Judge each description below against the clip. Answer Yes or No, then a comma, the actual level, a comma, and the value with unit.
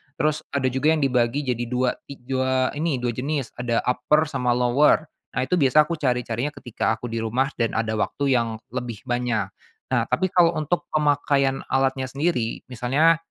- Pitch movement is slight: No, average, 3.4 semitones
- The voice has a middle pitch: No, low, 130 Hz